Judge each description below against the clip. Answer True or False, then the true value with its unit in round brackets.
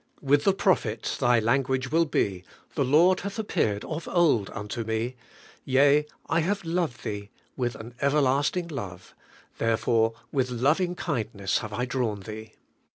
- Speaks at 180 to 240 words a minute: False (150 wpm)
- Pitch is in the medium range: False (130 Hz)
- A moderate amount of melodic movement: False (5.9 semitones)